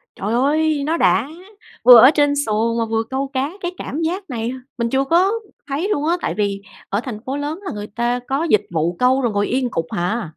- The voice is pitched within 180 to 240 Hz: No, very high, 255 Hz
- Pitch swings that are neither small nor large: Yes, average, 4.8 semitones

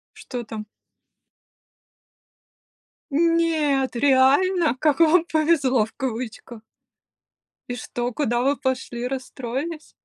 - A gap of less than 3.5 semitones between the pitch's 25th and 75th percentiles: No, average, 4.2 semitones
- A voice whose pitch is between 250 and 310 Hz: Yes, very high, 270 Hz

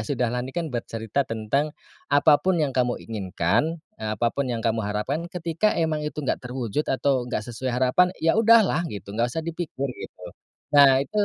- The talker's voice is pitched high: No, low, 130 Hz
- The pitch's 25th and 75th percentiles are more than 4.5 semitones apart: Yes, average, 5.1 semitones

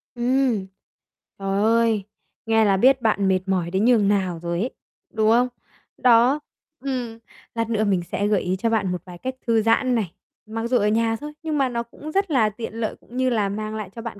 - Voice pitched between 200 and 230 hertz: Yes, high, 225 Hz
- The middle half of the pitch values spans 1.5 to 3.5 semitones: Yes, average, 3.2 semitones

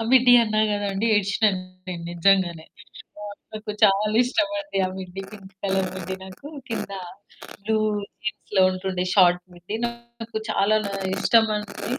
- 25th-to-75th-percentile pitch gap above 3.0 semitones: No, average, 2.7 semitones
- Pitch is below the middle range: No, high, 205 Hz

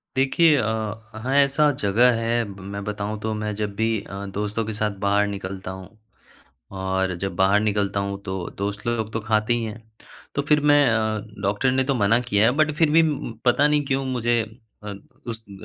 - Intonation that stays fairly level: No, average, 3.6 semitones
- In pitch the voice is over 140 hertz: No, low, 110 Hz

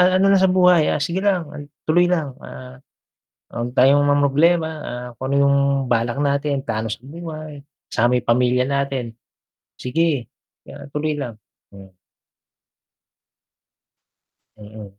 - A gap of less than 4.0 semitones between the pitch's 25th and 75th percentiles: No, average, 4.4 semitones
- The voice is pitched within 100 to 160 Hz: Yes, medium, 140 Hz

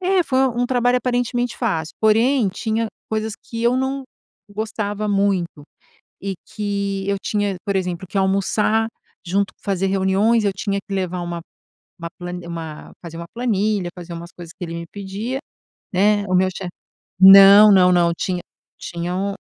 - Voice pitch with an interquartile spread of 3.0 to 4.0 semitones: Yes, average, 3.4 semitones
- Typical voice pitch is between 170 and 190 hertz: No, high, 200 Hz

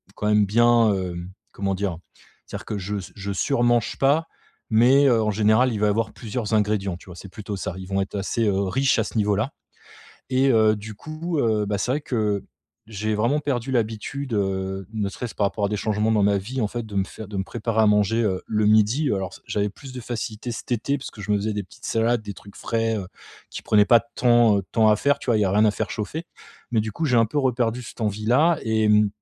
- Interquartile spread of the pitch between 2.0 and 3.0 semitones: Yes, average, 2.7 semitones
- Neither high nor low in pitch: No, low, 110 Hz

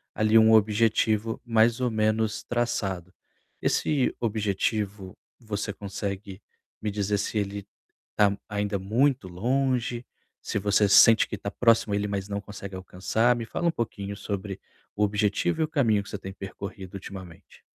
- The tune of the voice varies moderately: No, narrow, 2.3 semitones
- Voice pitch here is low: Yes, low, 105 Hz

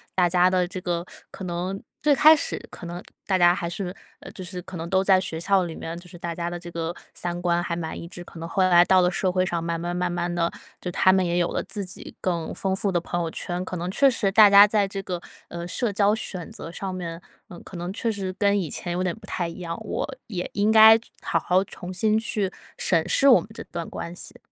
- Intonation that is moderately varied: No, narrow, 2.1 semitones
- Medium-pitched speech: Yes, medium, 180 Hz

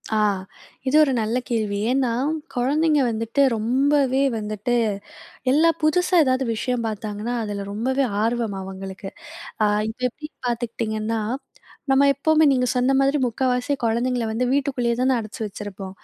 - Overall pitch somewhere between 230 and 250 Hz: Yes, high, 245 Hz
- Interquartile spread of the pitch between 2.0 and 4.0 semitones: Yes, average, 3.7 semitones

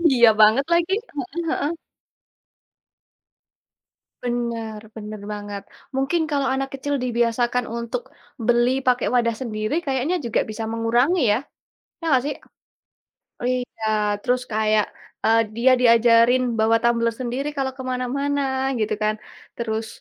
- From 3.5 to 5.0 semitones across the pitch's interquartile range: No, average, 2.8 semitones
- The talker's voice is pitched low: No, high, 240 Hz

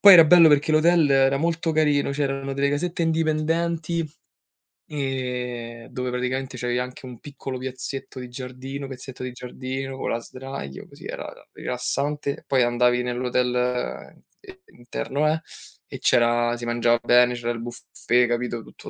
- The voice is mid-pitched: No, low, 130 Hz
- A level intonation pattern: No, average, 3.0 semitones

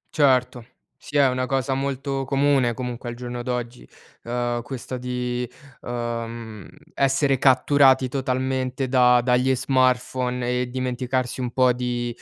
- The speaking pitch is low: Yes, low, 125 Hz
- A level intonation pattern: Yes, narrow, 1.4 semitones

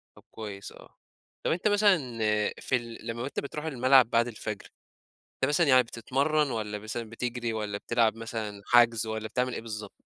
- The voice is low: Yes, low, 115 Hz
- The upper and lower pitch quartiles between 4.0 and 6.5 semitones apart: No, average, 2.9 semitones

